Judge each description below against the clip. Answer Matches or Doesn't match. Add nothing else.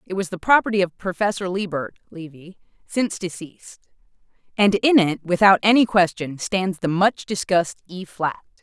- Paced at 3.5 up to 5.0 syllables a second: Doesn't match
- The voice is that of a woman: Matches